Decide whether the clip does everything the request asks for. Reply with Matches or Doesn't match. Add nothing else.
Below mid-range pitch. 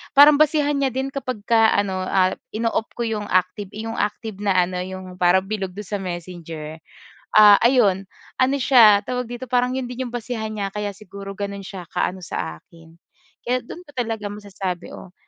Doesn't match